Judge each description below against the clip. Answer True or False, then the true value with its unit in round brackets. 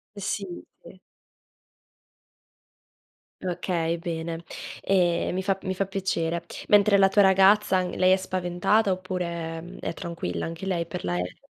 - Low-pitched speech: False (180 Hz)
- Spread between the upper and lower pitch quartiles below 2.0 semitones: False (2.3 semitones)